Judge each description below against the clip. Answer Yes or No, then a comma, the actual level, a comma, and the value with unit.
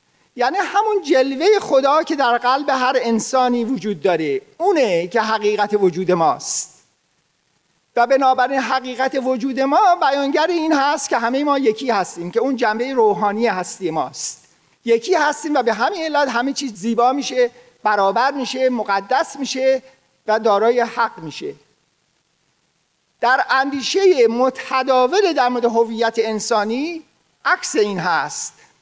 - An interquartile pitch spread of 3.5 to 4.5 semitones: Yes, average, 3.9 semitones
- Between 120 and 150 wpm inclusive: Yes, average, 130 wpm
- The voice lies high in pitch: Yes, very high, 255 Hz